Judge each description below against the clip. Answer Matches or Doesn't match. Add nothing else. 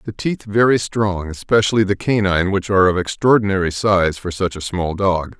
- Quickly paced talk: Doesn't match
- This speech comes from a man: Matches